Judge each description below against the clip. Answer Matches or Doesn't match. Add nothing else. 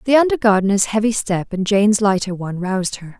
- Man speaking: Doesn't match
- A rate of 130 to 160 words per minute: Doesn't match